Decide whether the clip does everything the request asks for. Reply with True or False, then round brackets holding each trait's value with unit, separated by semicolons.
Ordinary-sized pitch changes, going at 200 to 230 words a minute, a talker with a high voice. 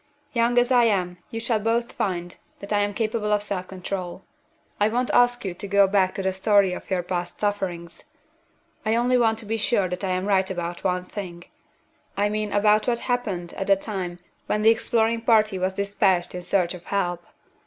True (3.3 semitones; 205 wpm; 200 Hz)